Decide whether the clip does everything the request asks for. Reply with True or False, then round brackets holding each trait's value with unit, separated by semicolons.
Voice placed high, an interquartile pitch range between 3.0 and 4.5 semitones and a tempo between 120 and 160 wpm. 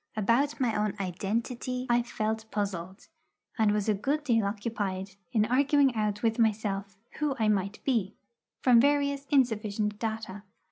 True (220 Hz; 3.4 semitones; 145 wpm)